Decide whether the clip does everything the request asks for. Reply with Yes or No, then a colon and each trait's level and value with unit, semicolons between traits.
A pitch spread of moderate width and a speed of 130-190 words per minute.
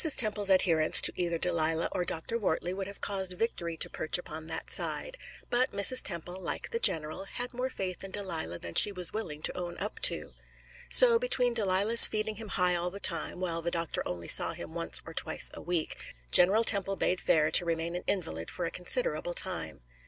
No: average, 3.8 semitones; fast, 205 wpm